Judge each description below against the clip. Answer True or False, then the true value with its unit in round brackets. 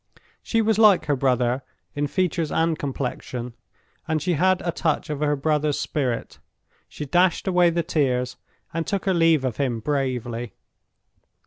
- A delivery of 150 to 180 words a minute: True (155 wpm)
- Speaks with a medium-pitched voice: True (150 Hz)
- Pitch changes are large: False (4.9 semitones)